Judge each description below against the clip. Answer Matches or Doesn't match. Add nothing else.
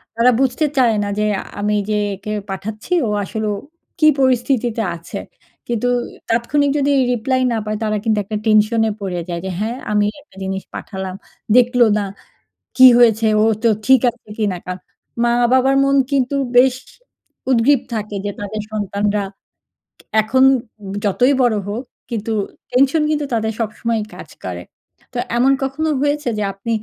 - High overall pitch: Matches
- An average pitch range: Matches